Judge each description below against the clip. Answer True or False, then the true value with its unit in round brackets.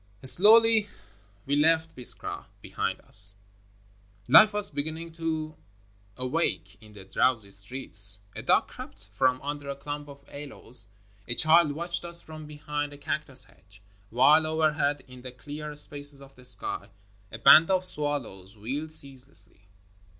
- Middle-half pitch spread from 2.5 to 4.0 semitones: False (4.7 semitones)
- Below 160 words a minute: True (150 wpm)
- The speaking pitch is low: False (145 Hz)